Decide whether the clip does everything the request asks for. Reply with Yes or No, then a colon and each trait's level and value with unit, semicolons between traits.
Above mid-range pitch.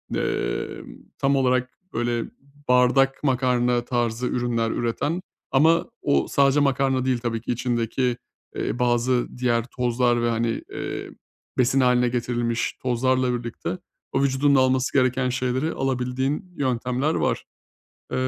No: low, 125 Hz